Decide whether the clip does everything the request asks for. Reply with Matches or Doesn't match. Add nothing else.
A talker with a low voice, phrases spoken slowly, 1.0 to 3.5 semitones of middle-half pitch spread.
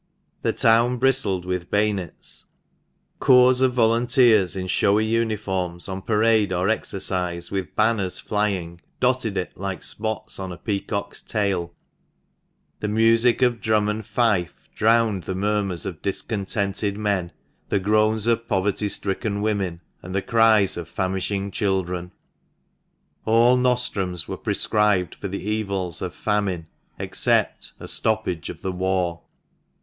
Matches